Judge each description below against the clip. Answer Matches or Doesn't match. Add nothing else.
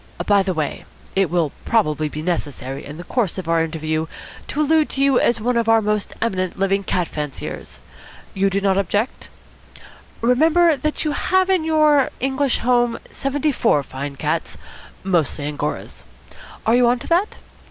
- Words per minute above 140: Matches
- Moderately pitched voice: Doesn't match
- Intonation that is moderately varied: Doesn't match